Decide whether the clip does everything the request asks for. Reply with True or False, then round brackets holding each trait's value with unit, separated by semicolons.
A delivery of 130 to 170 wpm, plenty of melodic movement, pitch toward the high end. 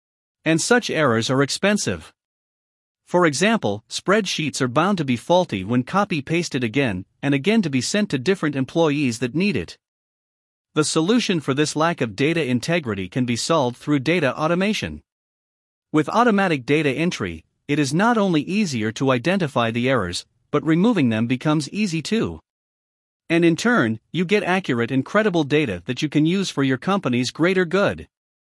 False (165 wpm; 6.2 semitones; 155 Hz)